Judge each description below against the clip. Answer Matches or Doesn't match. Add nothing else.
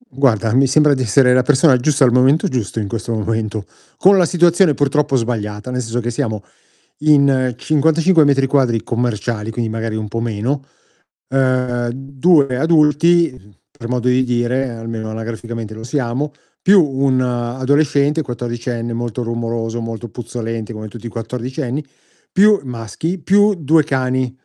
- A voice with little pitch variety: Doesn't match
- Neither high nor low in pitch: Doesn't match